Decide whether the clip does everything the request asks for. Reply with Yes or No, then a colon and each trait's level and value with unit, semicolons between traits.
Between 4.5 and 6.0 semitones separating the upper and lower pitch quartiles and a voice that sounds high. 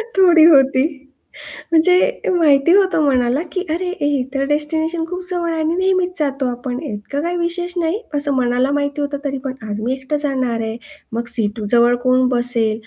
Yes: average, 5.1 semitones; very high, 285 Hz